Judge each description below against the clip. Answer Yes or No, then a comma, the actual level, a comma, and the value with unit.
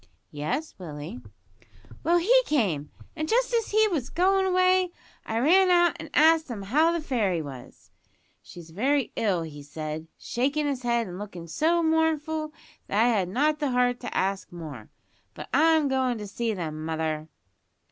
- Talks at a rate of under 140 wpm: No, average, 165 wpm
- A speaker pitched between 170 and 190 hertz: No, very high, 250 Hz